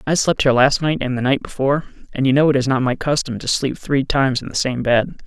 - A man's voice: Yes, male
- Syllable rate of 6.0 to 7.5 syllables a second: Yes, 6.4 syllables/s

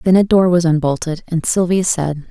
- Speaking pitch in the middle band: Yes, medium, 170 Hz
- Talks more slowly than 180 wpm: No, fast, 210 wpm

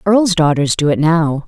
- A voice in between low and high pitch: Yes, medium, 165 Hz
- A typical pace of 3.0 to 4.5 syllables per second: Yes, 4.4 syllables/s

